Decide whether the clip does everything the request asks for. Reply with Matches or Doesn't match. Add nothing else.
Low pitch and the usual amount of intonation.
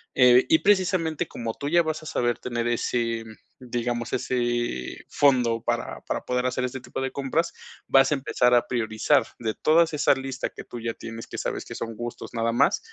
Matches